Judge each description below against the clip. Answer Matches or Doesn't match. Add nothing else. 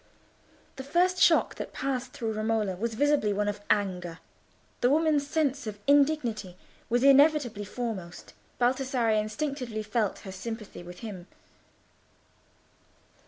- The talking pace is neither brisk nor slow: Doesn't match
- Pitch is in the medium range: Doesn't match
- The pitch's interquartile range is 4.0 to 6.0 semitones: Matches